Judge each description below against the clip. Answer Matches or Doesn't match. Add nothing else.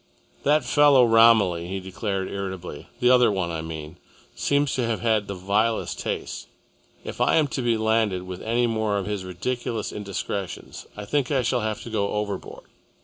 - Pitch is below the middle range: Matches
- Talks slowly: Doesn't match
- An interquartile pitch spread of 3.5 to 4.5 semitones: Matches